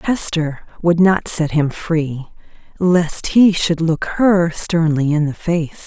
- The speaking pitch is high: No, medium, 165 Hz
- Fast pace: No, average, 155 wpm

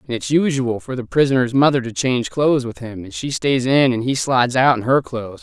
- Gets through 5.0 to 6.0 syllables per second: Yes, 5.9 syllables/s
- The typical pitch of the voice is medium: No, low, 130 Hz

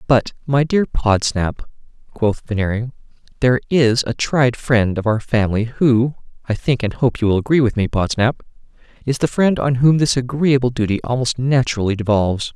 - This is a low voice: Yes, low, 120 Hz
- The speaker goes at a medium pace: Yes, average, 170 wpm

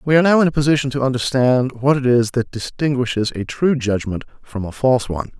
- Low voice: Yes, low, 130 Hz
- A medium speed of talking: No, fast, 220 wpm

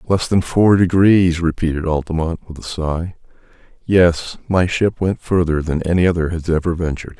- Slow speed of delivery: No, average, 165 wpm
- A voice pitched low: Yes, very low, 85 Hz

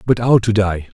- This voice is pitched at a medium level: No, low, 105 Hz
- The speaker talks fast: Yes, fast, 245 wpm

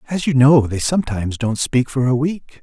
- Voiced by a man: Yes, male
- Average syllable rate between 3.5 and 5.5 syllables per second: Yes, 5.4 syllables/s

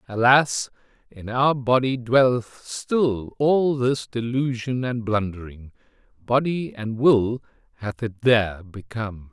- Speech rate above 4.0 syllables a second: No, 3.8 syllables/s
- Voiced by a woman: No, male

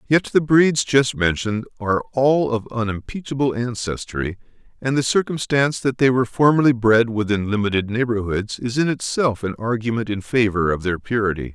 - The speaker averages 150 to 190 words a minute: Yes, average, 160 wpm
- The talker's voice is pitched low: Yes, low, 115 Hz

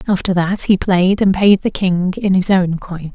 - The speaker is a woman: Yes, female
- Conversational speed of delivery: No, fast, 230 wpm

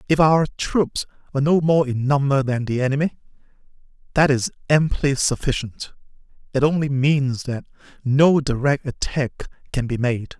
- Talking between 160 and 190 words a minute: No, average, 145 wpm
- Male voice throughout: Yes, male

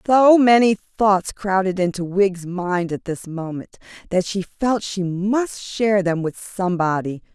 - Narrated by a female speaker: Yes, female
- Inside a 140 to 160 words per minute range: Yes, average, 155 wpm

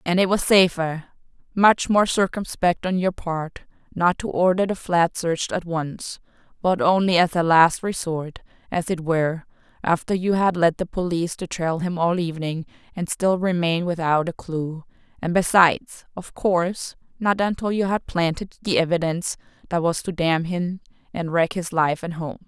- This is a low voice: No, medium, 175 Hz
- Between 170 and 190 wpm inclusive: Yes, average, 175 wpm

